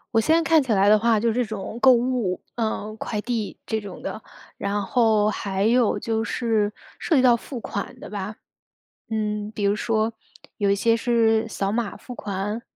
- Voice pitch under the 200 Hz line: No, high, 220 Hz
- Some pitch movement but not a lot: No, narrow, 2.2 semitones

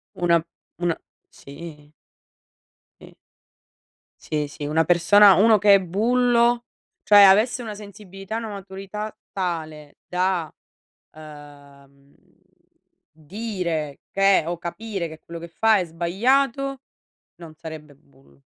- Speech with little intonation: No, average, 5.1 semitones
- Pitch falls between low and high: Yes, medium, 180 Hz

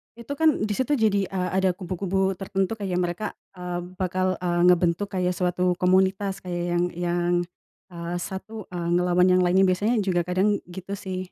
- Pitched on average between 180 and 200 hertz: Yes, medium, 185 Hz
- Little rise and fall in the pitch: Yes, narrow, 1.6 semitones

